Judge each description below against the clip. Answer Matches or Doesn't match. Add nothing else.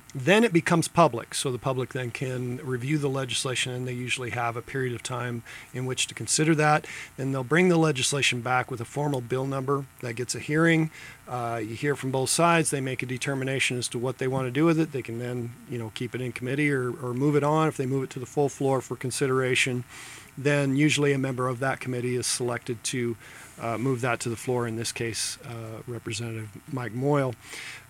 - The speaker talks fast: Matches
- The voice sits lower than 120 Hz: Doesn't match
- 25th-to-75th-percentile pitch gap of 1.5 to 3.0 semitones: Matches